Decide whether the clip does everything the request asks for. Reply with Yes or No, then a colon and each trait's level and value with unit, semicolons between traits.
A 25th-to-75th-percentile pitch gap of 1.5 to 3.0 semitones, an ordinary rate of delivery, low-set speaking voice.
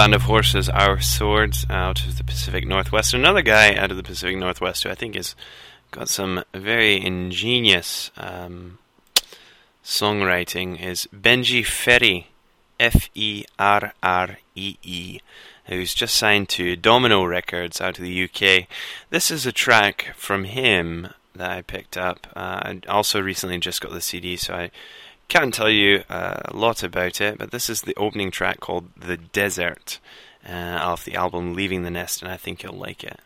Yes: average, 2.7 semitones; average, 175 wpm; very low, 90 Hz